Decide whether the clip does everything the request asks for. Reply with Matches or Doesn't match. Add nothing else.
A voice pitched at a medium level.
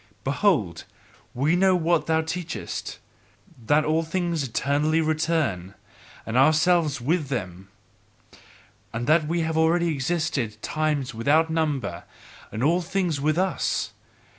Matches